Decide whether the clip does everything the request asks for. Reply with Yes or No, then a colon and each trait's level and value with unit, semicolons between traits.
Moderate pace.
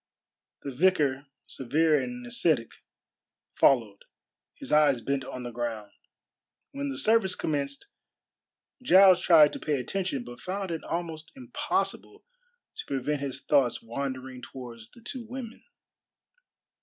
No: slow, 125 wpm